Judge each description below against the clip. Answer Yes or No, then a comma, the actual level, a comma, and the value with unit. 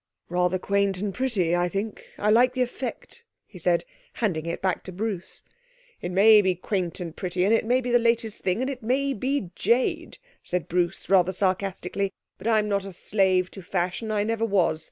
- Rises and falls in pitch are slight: No, average, 3.8 semitones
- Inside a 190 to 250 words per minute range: Yes, average, 195 wpm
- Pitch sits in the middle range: No, high, 200 Hz